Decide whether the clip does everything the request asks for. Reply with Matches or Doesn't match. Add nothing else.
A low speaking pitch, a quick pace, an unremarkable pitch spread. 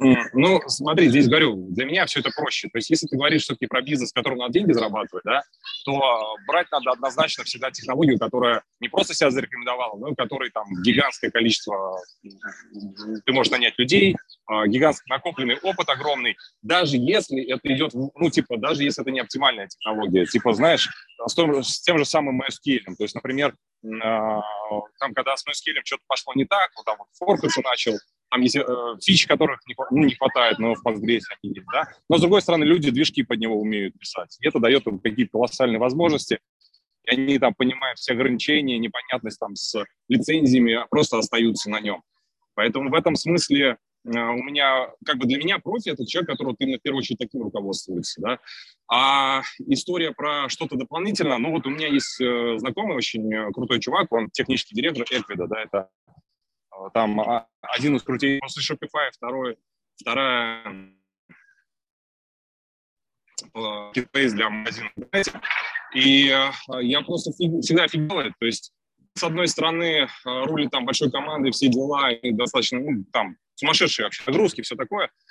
Matches